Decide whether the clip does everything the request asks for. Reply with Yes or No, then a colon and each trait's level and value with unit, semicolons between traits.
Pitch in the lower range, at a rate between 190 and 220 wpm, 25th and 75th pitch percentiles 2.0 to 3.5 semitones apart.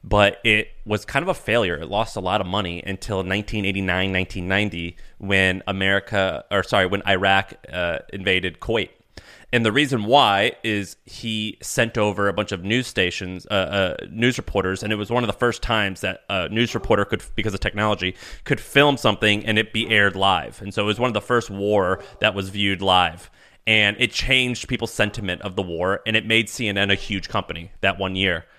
Yes: low, 105 Hz; fast, 205 wpm; narrow, 2.5 semitones